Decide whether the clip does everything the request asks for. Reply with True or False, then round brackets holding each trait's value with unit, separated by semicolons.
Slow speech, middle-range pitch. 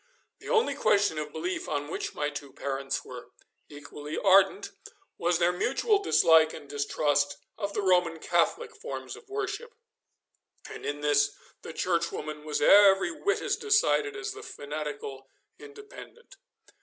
False (145 wpm; 170 Hz)